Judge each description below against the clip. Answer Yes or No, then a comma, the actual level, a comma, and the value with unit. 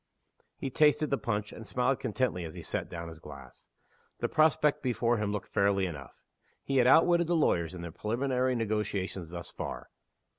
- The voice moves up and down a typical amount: No, wide, 6.3 semitones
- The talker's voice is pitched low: Yes, low, 110 Hz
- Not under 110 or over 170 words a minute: No, average, 180 wpm